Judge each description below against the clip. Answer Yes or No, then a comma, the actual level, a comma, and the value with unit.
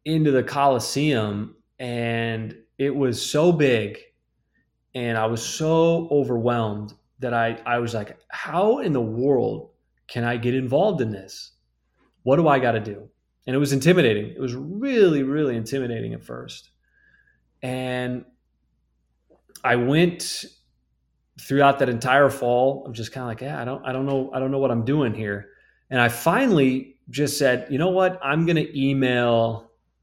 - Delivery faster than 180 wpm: No, average, 165 wpm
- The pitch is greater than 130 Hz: No, low, 125 Hz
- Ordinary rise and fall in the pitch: Yes, average, 3.6 semitones